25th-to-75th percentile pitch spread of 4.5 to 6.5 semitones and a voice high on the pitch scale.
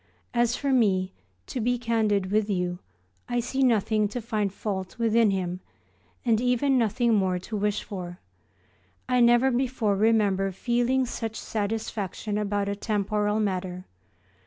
No: average, 3.3 semitones; high, 215 Hz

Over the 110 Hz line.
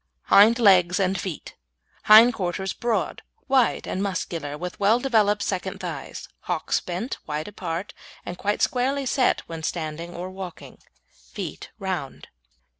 Yes: high, 190 Hz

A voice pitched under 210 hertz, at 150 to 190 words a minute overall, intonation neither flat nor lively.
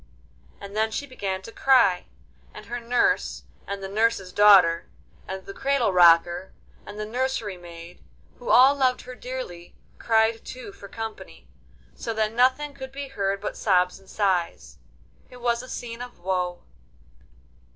No: high, 215 Hz; average, 155 wpm; average, 4.9 semitones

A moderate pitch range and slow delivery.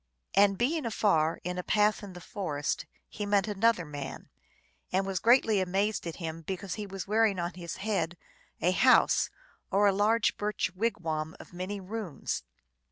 No: average, 3.2 semitones; average, 175 wpm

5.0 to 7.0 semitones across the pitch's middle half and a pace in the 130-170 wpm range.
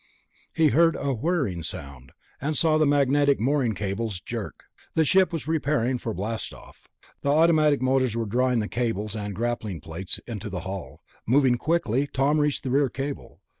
Yes: wide, 5.4 semitones; average, 165 wpm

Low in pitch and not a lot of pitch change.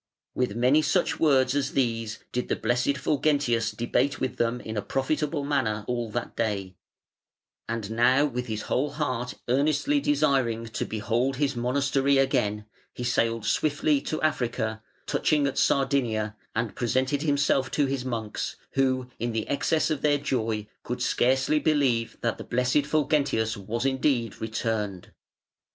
No: low, 130 Hz; average, 3.7 semitones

